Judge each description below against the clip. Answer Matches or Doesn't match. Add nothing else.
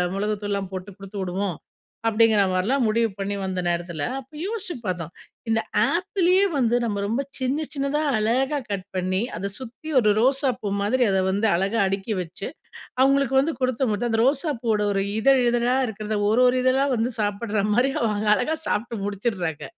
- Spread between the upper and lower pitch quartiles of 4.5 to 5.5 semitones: Matches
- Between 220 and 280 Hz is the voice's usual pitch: Matches